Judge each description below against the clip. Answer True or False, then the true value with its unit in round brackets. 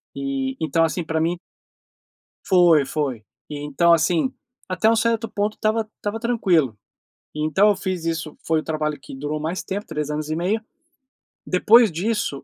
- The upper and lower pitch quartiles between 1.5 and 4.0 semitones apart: False (5.3 semitones)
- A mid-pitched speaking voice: True (165 Hz)